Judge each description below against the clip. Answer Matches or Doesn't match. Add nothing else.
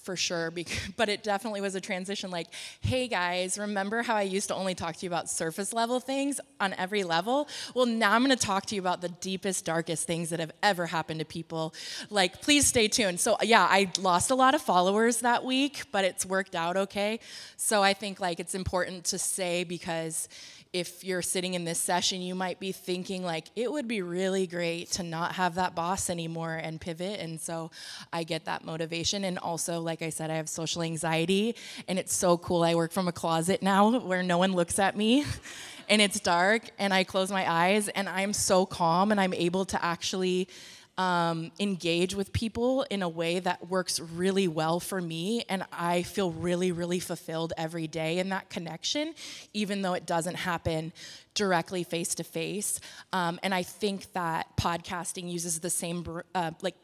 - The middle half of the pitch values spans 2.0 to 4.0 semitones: Matches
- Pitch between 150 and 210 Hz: Matches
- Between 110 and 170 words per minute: Doesn't match